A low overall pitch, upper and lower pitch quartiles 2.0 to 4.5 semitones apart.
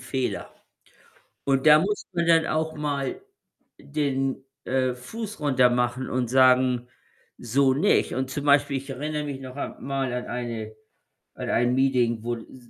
Yes: low, 130 Hz; narrow, 2.6 semitones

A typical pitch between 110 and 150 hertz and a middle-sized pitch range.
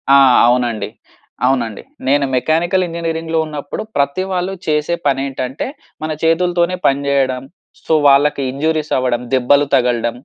Yes: medium, 140 Hz; average, 3.9 semitones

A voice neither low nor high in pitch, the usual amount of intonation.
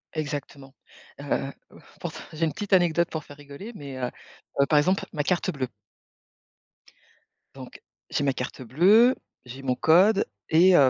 Yes: medium, 150 Hz; average, 4.5 semitones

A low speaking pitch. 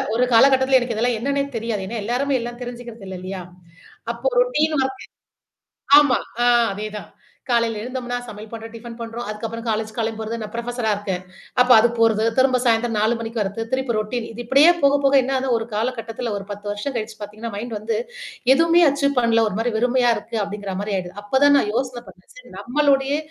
No: high, 235 Hz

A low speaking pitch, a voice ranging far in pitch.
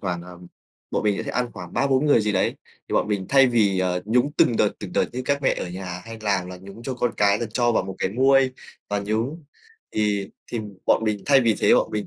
No: low, 105 Hz; average, 4.3 semitones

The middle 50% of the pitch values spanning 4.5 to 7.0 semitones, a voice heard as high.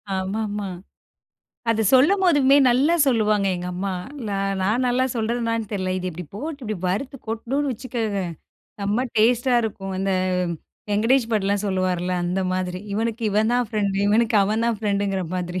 No: average, 3.7 semitones; high, 215 Hz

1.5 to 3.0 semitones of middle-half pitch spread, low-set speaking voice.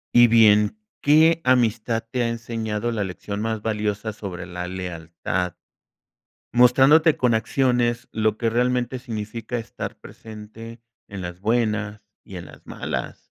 Yes: average, 2.7 semitones; low, 110 Hz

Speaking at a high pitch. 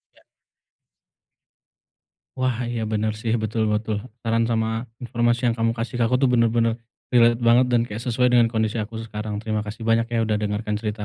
No: low, 115 Hz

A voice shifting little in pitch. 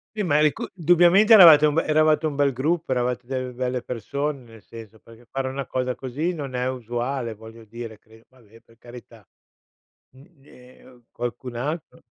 No: average, 4.0 semitones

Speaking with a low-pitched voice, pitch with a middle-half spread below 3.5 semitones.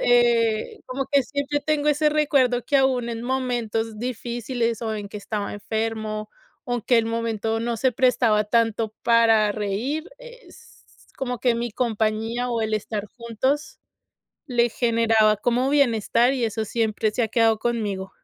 No: high, 230 Hz; narrow, 2.4 semitones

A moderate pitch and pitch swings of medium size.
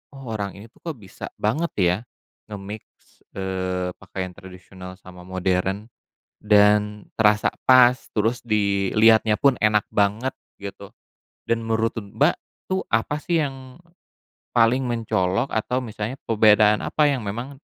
No: low, 105 Hz; average, 3.1 semitones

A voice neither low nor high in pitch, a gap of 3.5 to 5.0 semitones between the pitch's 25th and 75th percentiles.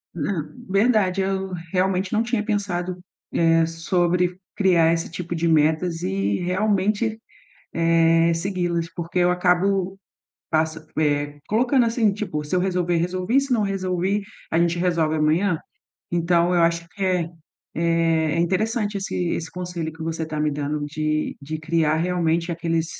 No: medium, 175 Hz; average, 2.7 semitones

